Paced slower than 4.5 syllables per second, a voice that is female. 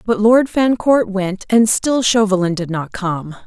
Yes: 4.0 syllables/s; female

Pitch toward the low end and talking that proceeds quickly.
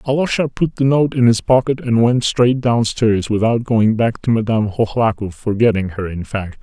No: low, 115 Hz; average, 190 wpm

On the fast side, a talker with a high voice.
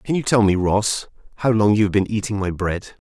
No: fast, 255 wpm; low, 105 Hz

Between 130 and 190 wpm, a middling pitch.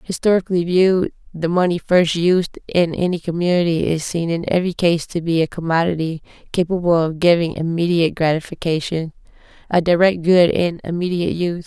Yes: average, 150 wpm; medium, 170 Hz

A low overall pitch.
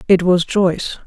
No: medium, 180 Hz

